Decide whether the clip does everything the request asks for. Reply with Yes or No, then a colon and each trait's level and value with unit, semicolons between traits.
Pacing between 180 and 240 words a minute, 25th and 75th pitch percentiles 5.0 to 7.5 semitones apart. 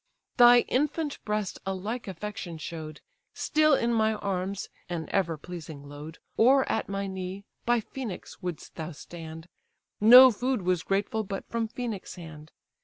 No: average, 150 wpm; wide, 5.5 semitones